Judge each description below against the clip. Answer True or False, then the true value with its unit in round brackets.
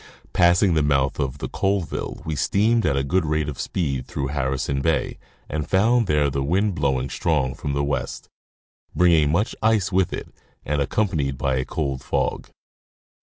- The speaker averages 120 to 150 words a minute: False (170 wpm)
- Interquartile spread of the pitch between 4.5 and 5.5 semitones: True (4.8 semitones)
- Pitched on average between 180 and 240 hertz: False (75 Hz)